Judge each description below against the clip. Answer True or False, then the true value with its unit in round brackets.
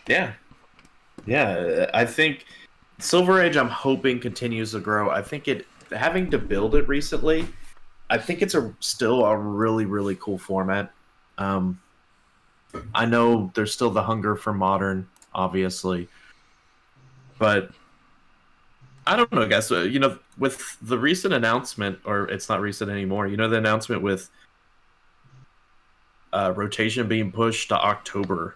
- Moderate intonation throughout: True (3.9 semitones)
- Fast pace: False (145 wpm)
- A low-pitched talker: True (110 Hz)